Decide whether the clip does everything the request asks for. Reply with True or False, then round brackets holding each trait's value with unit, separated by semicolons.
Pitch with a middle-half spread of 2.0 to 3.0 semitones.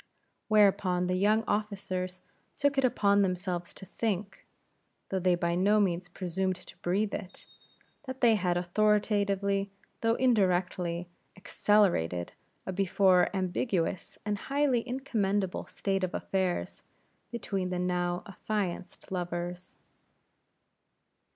True (2.6 semitones)